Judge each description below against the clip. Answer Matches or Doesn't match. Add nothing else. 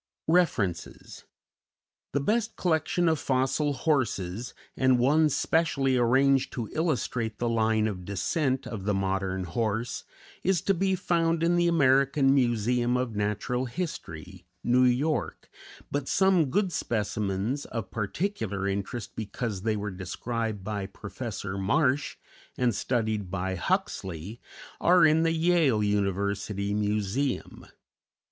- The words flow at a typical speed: Doesn't match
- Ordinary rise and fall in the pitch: Doesn't match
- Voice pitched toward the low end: Matches